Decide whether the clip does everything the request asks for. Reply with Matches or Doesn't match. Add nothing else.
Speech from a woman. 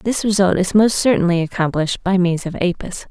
Matches